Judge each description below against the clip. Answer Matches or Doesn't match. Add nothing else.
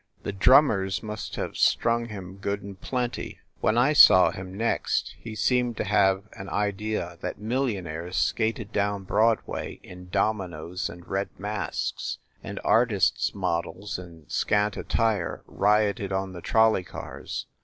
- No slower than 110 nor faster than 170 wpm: Matches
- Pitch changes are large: Doesn't match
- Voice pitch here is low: Matches